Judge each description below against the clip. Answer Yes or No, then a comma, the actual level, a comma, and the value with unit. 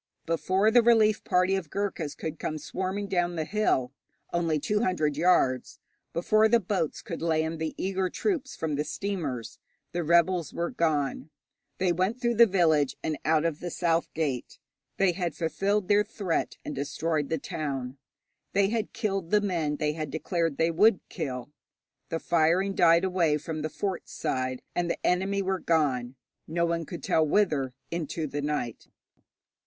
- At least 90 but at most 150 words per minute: No, average, 170 wpm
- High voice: No, medium, 170 Hz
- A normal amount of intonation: Yes, average, 4.1 semitones